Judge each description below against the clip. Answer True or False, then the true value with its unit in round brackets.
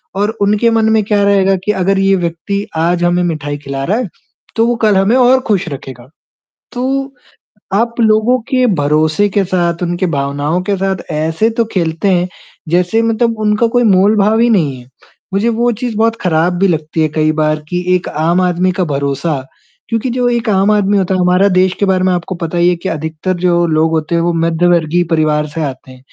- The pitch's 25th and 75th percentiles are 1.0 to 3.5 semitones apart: False (4.6 semitones)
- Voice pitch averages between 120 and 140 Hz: False (180 Hz)